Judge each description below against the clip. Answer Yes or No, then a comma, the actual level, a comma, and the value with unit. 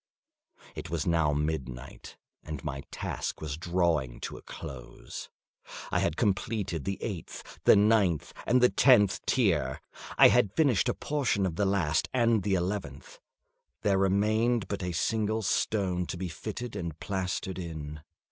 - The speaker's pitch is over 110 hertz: No, very low, 95 Hz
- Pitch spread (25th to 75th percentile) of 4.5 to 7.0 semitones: Yes, average, 5.0 semitones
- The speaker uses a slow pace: No, average, 150 wpm